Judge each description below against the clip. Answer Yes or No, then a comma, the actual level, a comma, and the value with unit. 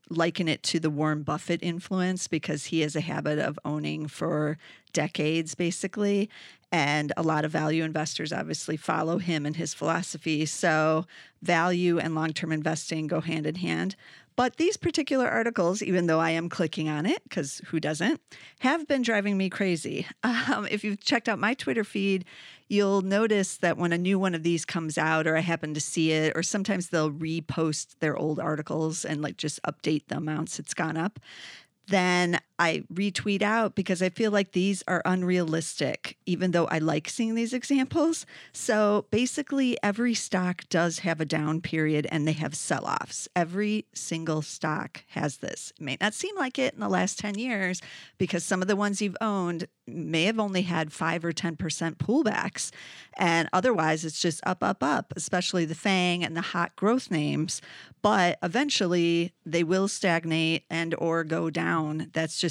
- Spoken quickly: No, average, 180 wpm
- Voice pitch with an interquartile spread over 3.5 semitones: Yes, average, 3.9 semitones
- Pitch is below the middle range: No, medium, 170 Hz